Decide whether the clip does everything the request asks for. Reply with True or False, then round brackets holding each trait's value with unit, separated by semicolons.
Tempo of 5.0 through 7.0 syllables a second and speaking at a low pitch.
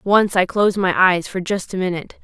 False (5.7 syllables/s; 190 Hz)